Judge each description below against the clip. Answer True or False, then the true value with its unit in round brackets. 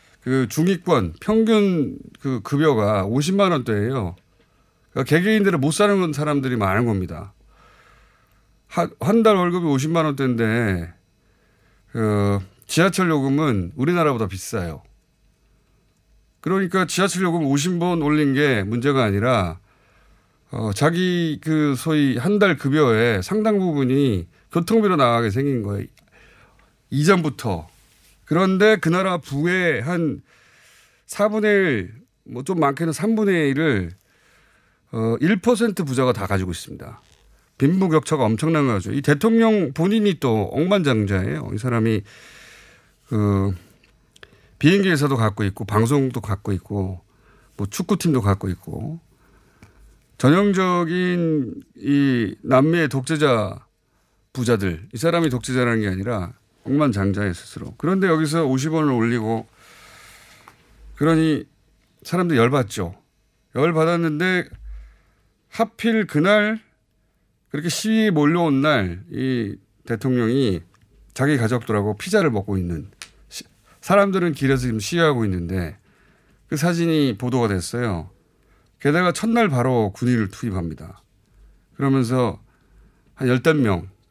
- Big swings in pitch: True (7.7 semitones)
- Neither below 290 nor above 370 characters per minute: False (245 characters per minute)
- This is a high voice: False (130 Hz)